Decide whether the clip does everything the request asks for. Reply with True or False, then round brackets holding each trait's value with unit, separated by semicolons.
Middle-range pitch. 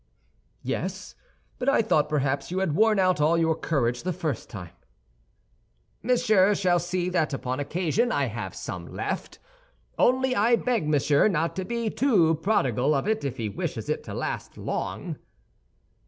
True (175 Hz)